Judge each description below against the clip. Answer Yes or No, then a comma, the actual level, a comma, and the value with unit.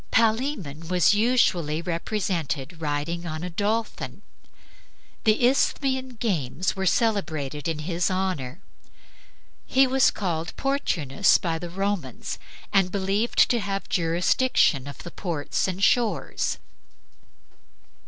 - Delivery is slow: Yes, slow, 110 wpm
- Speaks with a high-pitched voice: No, medium, 180 Hz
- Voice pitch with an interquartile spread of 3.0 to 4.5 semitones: No, average, 5.1 semitones